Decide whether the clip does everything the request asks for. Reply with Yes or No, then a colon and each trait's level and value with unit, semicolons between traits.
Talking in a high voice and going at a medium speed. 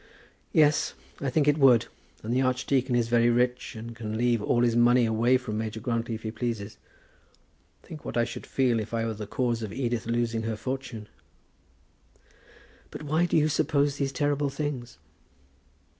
No: low, 120 Hz; average, 175 wpm